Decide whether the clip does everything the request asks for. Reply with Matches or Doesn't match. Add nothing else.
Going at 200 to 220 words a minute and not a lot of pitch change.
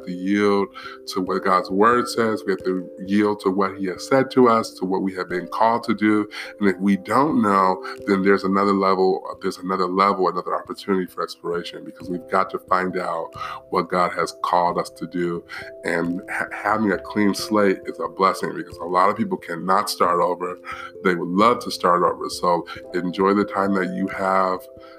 Matches